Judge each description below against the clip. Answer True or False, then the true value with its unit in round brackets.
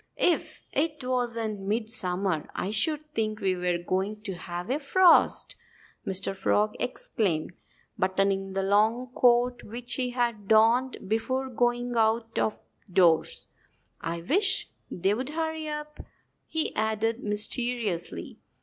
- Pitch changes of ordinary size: True (4.5 semitones)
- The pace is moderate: False (120 wpm)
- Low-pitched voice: False (225 Hz)